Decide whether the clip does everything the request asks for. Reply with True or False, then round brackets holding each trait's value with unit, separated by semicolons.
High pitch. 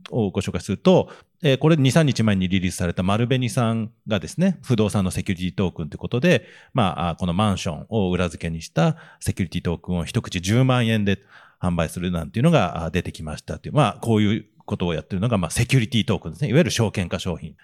False (100 Hz)